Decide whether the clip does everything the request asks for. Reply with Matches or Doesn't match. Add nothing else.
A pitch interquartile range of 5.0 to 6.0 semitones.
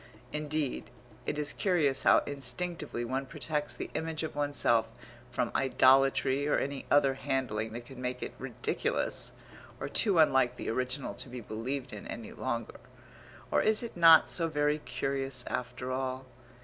Doesn't match